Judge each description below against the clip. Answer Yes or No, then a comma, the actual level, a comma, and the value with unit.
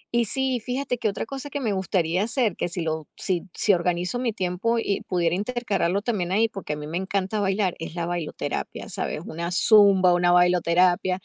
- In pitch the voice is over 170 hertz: Yes, high, 190 Hz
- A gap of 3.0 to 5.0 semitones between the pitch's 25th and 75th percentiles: Yes, average, 4.1 semitones